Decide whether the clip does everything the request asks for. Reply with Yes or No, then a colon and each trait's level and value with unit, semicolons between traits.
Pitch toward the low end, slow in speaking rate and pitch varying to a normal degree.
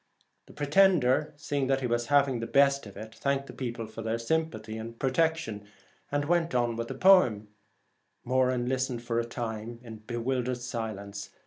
No: low, 125 Hz; average, 180 wpm; average, 3.4 semitones